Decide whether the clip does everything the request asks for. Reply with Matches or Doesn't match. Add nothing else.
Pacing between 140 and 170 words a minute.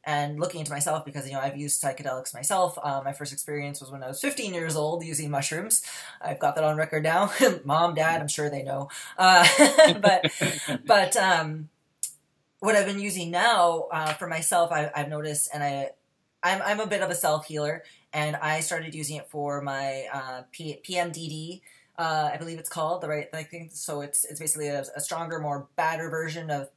Doesn't match